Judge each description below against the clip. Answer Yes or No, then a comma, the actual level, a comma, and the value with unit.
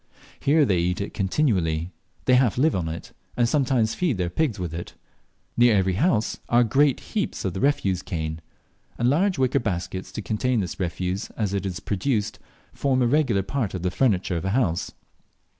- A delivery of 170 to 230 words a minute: Yes, average, 190 wpm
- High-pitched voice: No, low, 105 Hz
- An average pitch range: No, wide, 6.1 semitones